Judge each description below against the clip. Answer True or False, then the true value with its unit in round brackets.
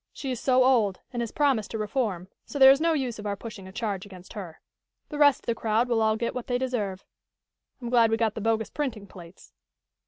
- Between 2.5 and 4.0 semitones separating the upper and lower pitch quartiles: True (3.7 semitones)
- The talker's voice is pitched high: True (225 Hz)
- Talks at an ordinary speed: False (240 wpm)